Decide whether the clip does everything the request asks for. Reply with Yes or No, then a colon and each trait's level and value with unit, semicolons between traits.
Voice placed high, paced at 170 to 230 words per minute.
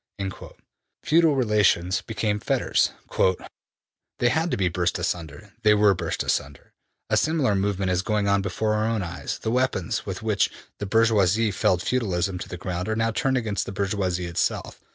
No: low, 100 Hz; average, 175 wpm